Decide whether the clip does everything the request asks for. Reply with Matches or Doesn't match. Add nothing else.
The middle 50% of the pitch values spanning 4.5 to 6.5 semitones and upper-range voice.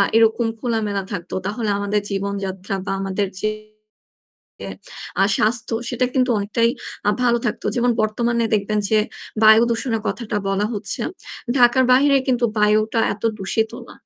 Doesn't match